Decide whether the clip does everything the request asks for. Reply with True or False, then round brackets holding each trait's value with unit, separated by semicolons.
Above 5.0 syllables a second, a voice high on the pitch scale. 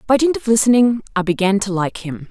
True (5.9 syllables/s; 210 Hz)